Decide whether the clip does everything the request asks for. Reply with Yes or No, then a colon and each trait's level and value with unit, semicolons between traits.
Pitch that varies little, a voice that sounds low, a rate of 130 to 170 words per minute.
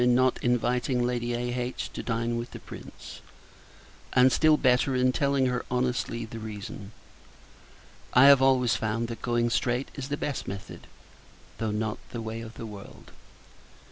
Yes: narrow, 1.8 semitones; low, 120 Hz; average, 160 wpm